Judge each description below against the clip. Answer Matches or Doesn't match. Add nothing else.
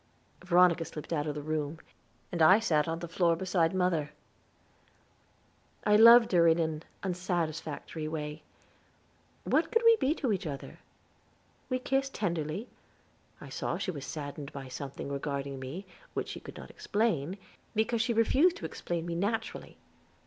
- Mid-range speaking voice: Matches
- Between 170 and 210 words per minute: Doesn't match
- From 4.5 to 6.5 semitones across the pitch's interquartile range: Matches